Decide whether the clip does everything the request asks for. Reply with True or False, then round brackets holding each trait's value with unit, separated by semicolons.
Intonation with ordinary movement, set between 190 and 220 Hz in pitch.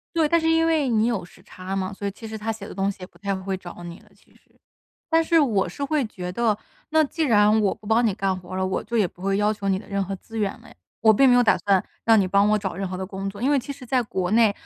True (3.8 semitones; 210 Hz)